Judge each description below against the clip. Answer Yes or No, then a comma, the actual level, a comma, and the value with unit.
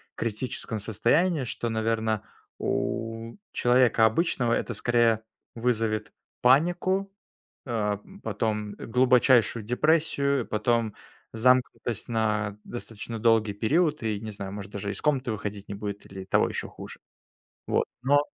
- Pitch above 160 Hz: No, low, 115 Hz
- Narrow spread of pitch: No, average, 3.0 semitones